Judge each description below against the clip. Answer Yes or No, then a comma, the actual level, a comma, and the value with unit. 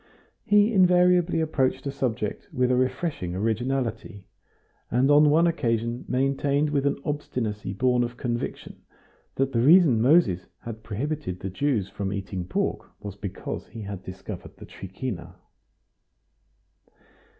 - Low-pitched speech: Yes, low, 125 Hz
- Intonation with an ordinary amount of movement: No, wide, 5.8 semitones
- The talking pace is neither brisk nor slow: No, slow, 130 wpm